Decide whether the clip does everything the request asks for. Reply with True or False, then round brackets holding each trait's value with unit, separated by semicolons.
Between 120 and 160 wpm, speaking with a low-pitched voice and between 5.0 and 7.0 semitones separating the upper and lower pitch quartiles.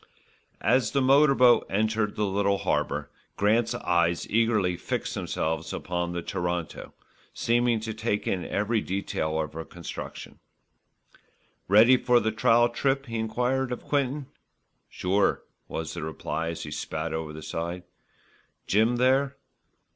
True (140 wpm; 105 Hz; 5.6 semitones)